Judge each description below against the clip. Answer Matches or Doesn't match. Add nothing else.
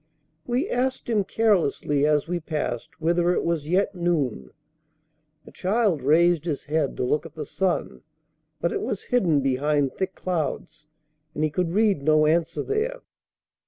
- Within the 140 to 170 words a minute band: Matches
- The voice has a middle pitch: Matches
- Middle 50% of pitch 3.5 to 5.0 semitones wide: Matches